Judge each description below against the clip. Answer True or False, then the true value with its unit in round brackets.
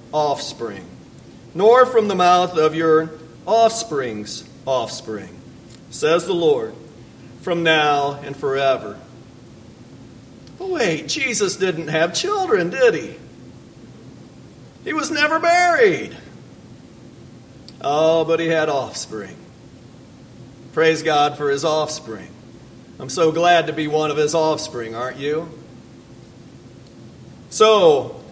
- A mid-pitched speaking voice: True (155 Hz)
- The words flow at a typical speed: False (105 wpm)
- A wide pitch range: True (7.1 semitones)